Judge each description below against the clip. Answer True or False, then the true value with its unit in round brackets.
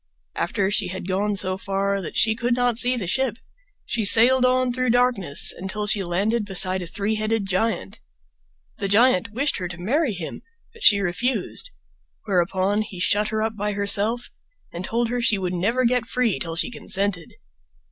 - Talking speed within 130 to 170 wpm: False (180 wpm)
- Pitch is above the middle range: True (210 Hz)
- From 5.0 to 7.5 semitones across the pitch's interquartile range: False (4.0 semitones)